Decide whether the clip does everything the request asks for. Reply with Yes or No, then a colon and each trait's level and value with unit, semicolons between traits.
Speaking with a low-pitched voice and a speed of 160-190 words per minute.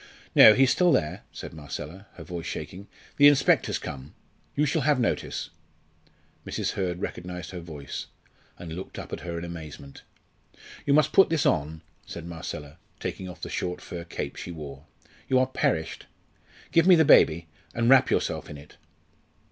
Yes: very low, 90 Hz; average, 170 wpm